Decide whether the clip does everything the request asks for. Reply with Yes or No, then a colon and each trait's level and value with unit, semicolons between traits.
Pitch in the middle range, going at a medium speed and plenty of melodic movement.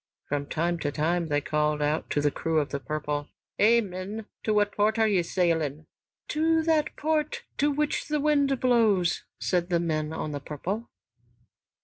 Yes: medium, 175 Hz; average, 170 wpm; wide, 7.6 semitones